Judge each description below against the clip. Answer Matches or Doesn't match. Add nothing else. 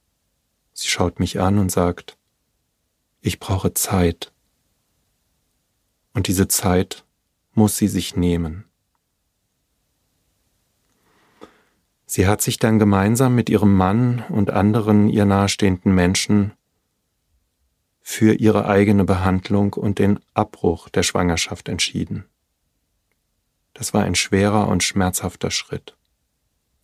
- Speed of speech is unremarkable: Doesn't match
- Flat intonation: Matches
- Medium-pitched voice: Doesn't match